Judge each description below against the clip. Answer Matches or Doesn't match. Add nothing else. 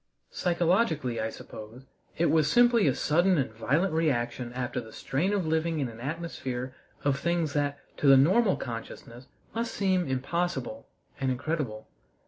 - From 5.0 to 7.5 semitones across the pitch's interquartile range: Matches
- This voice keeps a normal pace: Matches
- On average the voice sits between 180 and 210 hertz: Doesn't match